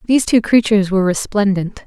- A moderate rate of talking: Yes, average, 160 wpm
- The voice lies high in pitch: Yes, high, 205 Hz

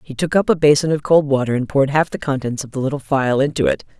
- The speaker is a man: No, female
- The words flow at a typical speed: No, fast, 285 wpm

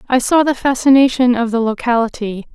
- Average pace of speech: Yes, average, 165 wpm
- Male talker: No, female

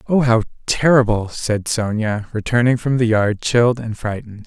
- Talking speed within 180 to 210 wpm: No, average, 160 wpm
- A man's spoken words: Yes, male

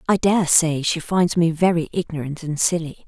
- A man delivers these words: No, female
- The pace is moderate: Yes, average, 195 wpm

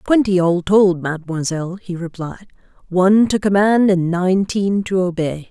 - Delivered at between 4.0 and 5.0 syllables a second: Yes, 4.8 syllables/s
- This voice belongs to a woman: Yes, female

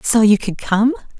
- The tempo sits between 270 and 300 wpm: No, average, 200 wpm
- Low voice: No, high, 215 Hz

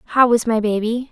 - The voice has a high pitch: Yes, high, 230 Hz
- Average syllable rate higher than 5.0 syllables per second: No, 4.7 syllables/s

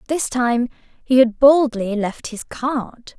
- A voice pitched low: No, very high, 250 Hz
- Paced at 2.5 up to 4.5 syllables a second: Yes, 3.4 syllables/s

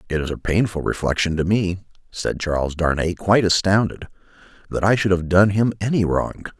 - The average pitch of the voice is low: Yes, very low, 90 Hz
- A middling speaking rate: Yes, average, 180 wpm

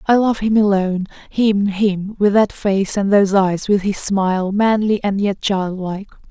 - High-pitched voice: Yes, high, 200 Hz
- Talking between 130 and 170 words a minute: No, average, 180 wpm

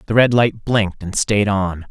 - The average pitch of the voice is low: Yes, low, 105 Hz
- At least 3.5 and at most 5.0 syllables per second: Yes, 4.7 syllables/s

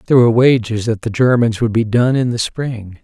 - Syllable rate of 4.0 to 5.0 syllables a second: No, 5.6 syllables/s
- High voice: No, low, 115 Hz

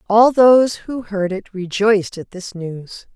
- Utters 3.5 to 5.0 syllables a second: Yes, 4.0 syllables/s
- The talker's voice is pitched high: Yes, high, 205 Hz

